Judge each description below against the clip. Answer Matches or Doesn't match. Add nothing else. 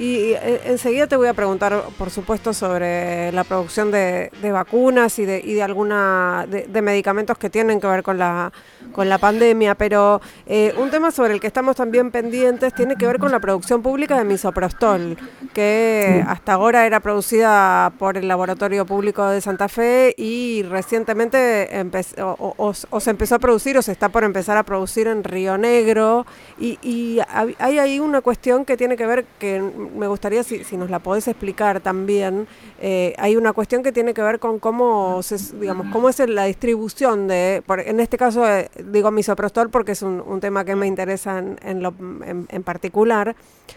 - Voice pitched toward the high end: Matches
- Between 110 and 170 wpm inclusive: Doesn't match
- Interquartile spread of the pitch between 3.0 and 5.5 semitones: Matches